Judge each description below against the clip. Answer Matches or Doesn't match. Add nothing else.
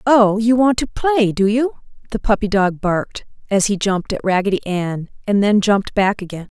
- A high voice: Matches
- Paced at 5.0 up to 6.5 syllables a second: Matches